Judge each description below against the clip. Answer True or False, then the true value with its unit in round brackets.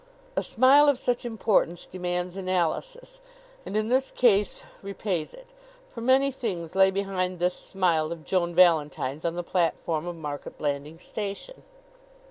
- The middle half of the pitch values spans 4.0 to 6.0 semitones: True (5.3 semitones)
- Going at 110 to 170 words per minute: True (145 wpm)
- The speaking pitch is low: False (185 Hz)